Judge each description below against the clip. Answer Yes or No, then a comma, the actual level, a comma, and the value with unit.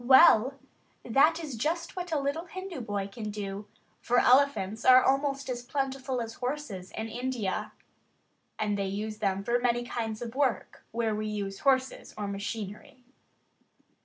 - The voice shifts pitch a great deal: No, average, 4.5 semitones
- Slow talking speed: No, average, 155 wpm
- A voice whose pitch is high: Yes, high, 240 Hz